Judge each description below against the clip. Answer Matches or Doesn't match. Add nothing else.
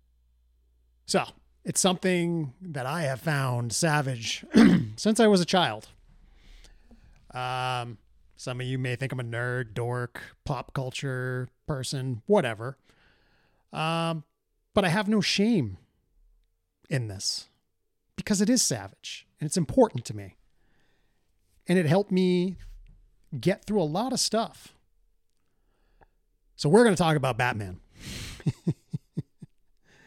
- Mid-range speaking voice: Doesn't match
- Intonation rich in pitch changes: Matches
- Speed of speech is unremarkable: Doesn't match